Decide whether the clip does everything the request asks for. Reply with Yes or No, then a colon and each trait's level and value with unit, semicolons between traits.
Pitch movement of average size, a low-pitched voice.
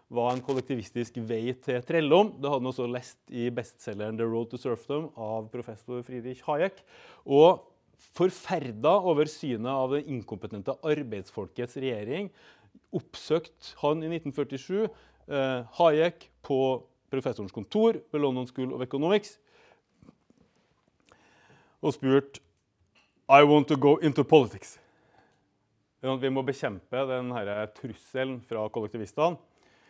Yes: average, 3.9 semitones; low, 130 Hz